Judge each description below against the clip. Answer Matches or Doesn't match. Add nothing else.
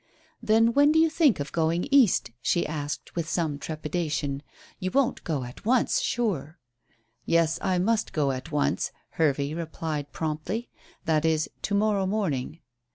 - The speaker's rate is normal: Matches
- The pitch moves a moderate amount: Doesn't match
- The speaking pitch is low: Doesn't match